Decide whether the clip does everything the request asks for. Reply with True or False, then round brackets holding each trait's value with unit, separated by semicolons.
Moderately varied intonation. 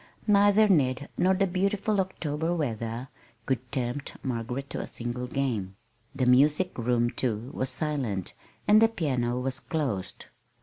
False (6.3 semitones)